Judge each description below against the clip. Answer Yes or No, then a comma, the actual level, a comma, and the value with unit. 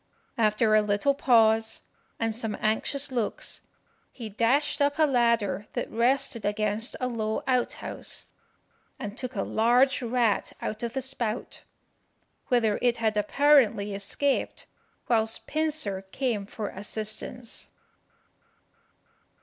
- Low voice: No, high, 230 Hz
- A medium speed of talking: No, slow, 120 wpm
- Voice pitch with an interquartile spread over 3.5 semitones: No, average, 3.0 semitones